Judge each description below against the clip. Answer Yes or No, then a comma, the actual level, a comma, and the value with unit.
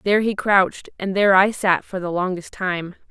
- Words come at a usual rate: No, fast, 215 wpm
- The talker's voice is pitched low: No, high, 190 Hz